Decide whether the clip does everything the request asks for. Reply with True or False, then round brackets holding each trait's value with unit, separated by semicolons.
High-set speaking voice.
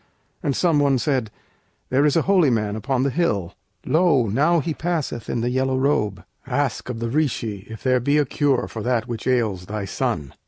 False (130 Hz)